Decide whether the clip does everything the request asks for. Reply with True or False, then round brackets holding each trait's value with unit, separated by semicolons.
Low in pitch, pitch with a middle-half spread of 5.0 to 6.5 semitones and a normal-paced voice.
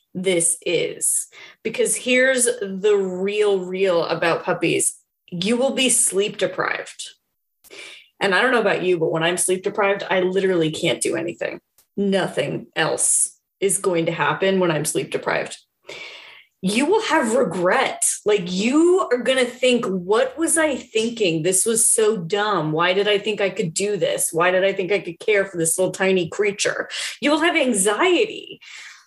False (200 Hz; 5.5 semitones; 170 wpm)